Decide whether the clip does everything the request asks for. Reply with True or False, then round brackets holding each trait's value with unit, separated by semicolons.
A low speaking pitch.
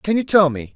False (175 Hz)